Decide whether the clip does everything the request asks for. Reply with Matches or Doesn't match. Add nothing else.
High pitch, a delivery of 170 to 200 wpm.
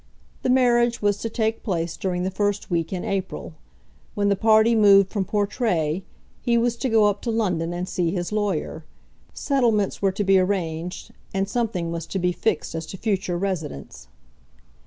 Matches